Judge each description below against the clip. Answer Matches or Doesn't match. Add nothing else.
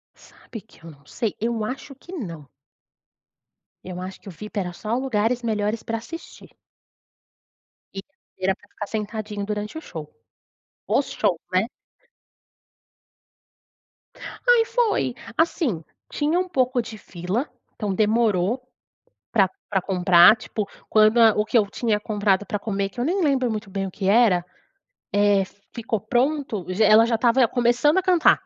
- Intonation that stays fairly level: Doesn't match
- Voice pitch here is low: Doesn't match